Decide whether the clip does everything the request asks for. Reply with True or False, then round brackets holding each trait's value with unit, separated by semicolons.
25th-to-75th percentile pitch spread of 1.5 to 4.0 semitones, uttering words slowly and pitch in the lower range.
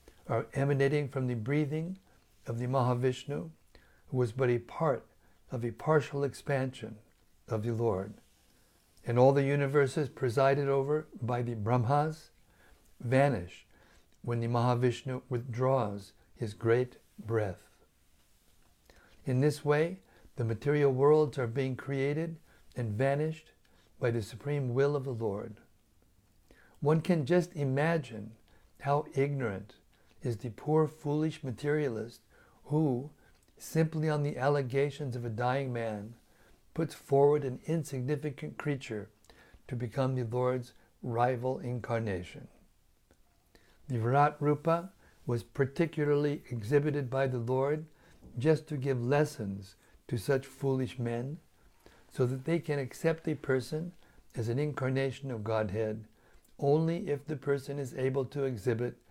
True (3.7 semitones; 125 wpm; 130 Hz)